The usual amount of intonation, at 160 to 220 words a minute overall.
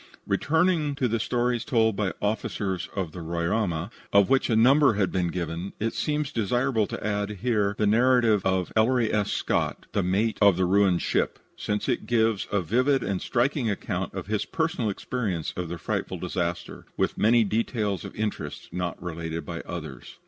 Yes: average, 4.5 semitones; average, 180 wpm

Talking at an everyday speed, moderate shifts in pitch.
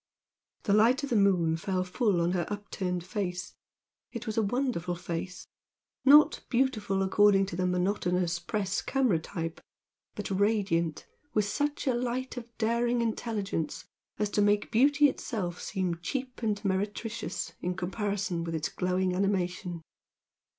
Yes: average, 145 wpm; average, 4.3 semitones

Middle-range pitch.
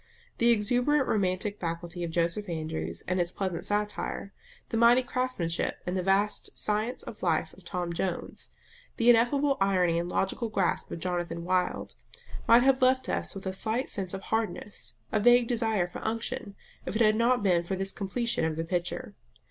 No: high, 200 Hz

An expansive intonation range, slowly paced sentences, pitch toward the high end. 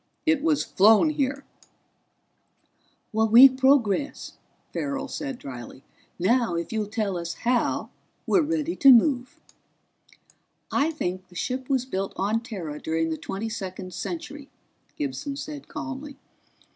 Yes: wide, 6.7 semitones; slow, 125 wpm; high, 245 Hz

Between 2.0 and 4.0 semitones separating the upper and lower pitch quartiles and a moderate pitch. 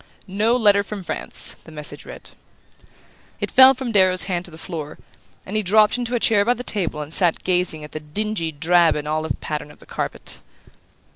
No: average, 5.3 semitones; medium, 180 Hz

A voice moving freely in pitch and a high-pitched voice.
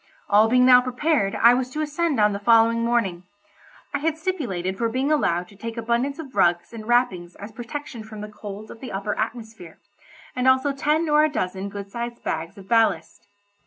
No: average, 4.4 semitones; high, 230 Hz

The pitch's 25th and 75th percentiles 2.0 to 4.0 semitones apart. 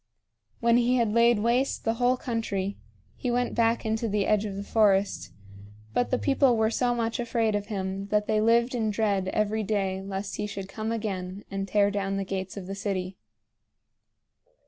Yes: average, 2.9 semitones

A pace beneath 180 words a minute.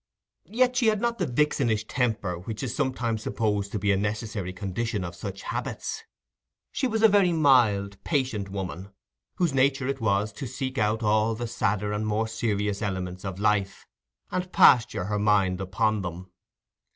Yes: average, 170 wpm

